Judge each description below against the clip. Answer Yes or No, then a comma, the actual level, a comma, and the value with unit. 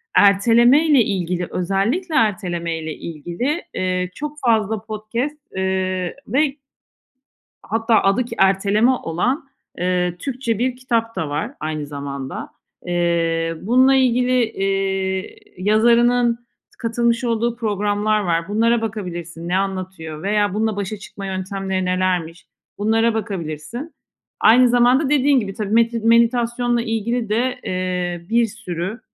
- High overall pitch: Yes, high, 210 Hz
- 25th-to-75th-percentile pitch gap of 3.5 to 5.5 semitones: Yes, average, 4.5 semitones